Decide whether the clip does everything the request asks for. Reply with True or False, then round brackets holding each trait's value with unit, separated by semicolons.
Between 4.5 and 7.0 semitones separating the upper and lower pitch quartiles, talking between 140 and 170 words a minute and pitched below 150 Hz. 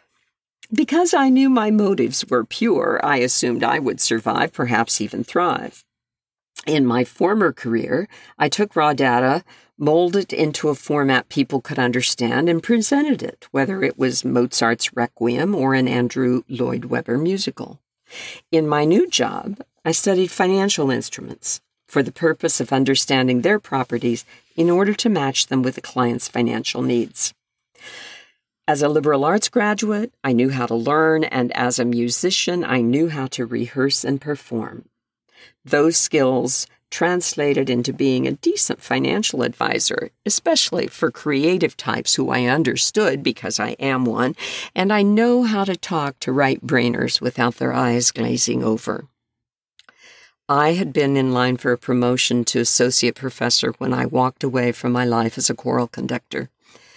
True (5.3 semitones; 155 wpm; 135 Hz)